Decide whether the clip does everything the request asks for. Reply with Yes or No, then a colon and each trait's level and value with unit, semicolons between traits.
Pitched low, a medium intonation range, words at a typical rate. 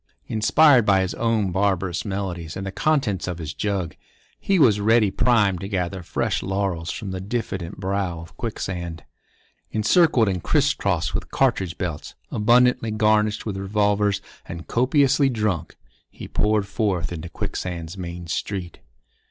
Yes: low, 100 Hz; average, 3.5 semitones; average, 145 wpm